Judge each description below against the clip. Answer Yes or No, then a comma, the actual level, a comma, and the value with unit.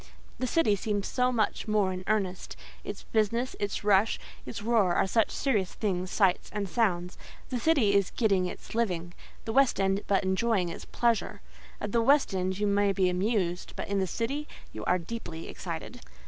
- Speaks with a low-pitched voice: No, high, 205 Hz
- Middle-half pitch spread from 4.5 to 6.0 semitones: No, average, 3.6 semitones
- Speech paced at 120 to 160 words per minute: No, average, 180 wpm